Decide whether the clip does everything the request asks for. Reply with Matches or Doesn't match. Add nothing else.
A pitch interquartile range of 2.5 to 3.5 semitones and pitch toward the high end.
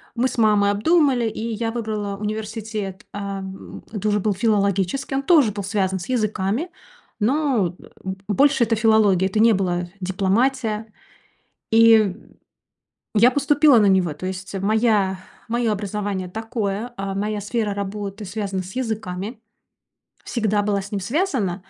Matches